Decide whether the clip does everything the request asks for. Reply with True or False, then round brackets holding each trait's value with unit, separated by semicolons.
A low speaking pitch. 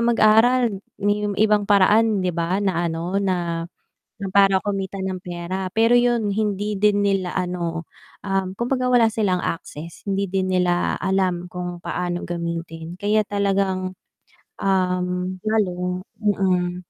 False (190 Hz)